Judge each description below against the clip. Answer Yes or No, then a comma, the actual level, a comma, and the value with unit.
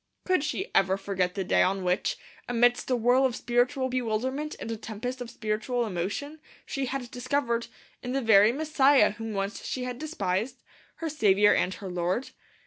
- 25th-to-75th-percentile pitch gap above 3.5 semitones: Yes, average, 4.4 semitones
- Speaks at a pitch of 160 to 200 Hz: No, high, 240 Hz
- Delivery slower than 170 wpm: No, average, 175 wpm